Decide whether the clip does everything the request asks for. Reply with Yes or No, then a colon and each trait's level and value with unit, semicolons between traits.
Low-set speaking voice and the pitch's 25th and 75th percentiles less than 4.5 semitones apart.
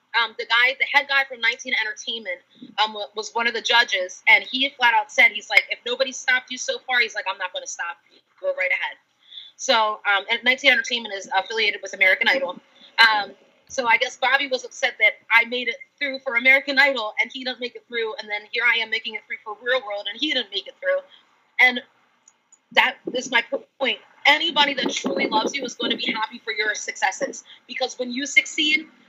No: high, 245 Hz; average, 3.7 semitones